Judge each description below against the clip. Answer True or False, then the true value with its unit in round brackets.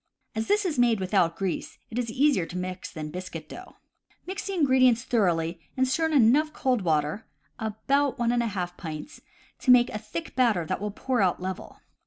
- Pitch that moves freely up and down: True (6.1 semitones)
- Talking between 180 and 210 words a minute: True (200 wpm)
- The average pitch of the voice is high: True (220 Hz)